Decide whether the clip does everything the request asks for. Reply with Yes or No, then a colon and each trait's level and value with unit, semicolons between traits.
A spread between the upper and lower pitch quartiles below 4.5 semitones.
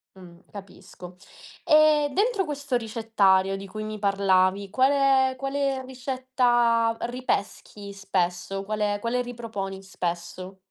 No: average, 5.1 semitones